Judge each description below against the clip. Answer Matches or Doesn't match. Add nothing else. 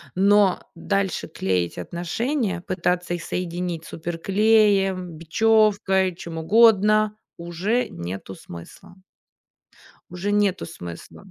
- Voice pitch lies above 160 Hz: Matches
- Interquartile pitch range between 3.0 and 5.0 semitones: Matches